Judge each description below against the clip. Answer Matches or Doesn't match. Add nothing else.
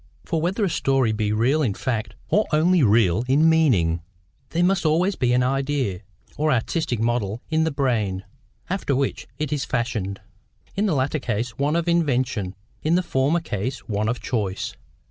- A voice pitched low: Matches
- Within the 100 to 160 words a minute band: Doesn't match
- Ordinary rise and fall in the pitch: Doesn't match